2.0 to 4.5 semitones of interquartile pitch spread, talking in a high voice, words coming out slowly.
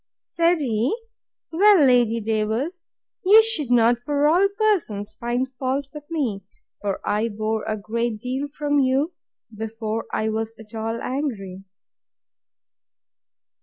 No: average, 5.2 semitones; high, 245 Hz; slow, 130 wpm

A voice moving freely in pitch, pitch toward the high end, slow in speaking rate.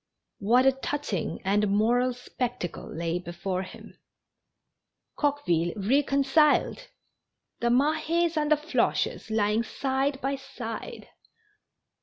Yes: wide, 5.8 semitones; very high, 250 Hz; slow, 105 wpm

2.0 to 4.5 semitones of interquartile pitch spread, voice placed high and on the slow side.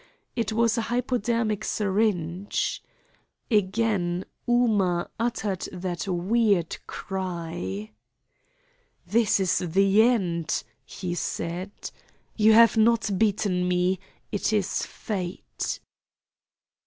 Yes: average, 3.8 semitones; high, 195 Hz; slow, 90 wpm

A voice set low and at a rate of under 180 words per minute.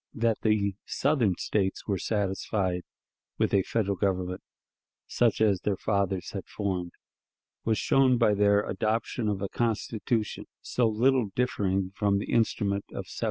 Yes: low, 105 Hz; average, 145 wpm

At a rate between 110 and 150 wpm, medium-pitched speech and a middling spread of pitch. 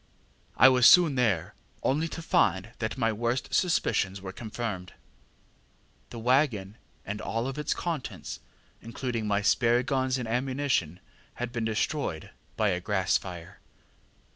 No: slow, 135 wpm; low, 115 Hz; average, 4.6 semitones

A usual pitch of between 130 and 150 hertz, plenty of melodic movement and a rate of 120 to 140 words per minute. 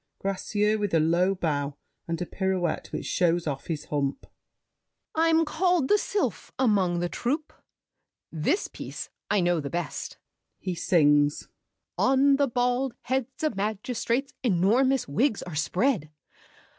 No: high, 195 Hz; wide, 7.8 semitones; slow, 135 wpm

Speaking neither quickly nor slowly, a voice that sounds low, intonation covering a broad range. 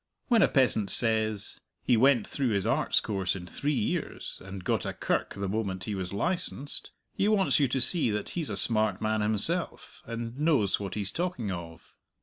Yes: average, 190 wpm; low, 110 Hz; wide, 6.0 semitones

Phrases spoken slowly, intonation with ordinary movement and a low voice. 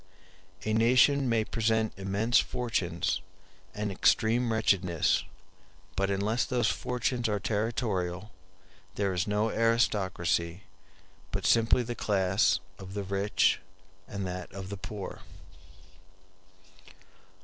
Yes: slow, 105 wpm; average, 3.0 semitones; low, 105 Hz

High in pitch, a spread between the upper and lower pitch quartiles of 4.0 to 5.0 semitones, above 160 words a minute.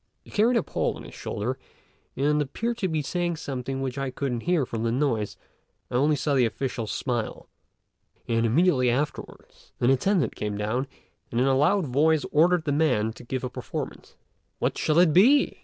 No: low, 135 Hz; average, 4.6 semitones; average, 190 wpm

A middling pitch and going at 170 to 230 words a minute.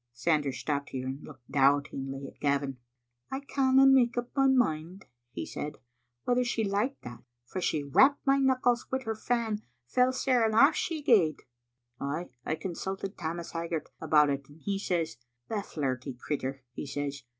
Yes: medium, 165 Hz; average, 185 wpm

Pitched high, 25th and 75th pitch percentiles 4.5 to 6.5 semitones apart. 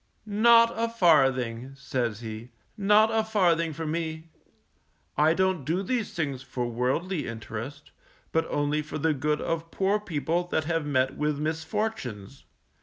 No: medium, 155 Hz; average, 5.3 semitones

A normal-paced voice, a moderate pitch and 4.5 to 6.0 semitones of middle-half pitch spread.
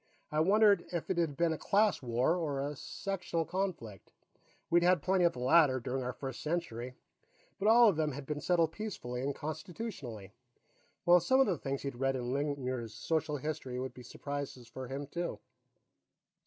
Yes: average, 180 wpm; medium, 150 Hz; average, 5.1 semitones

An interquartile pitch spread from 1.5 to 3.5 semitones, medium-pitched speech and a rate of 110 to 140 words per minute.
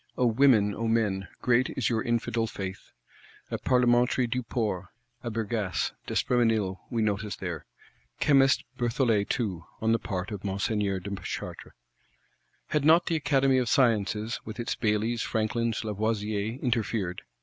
No: average, 2.8 semitones; low, 115 Hz; slow, 135 wpm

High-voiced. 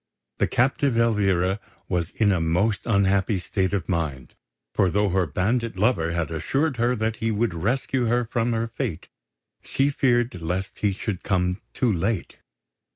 No: low, 105 Hz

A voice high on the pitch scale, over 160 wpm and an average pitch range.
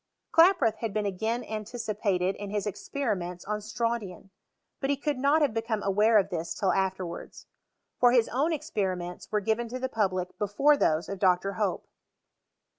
Yes: high, 215 Hz; average, 175 wpm; average, 4.0 semitones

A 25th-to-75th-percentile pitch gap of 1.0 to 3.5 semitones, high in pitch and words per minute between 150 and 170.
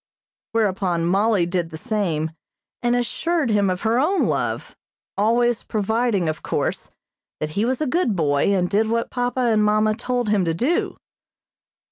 No: average, 4.9 semitones; high, 215 Hz; average, 160 wpm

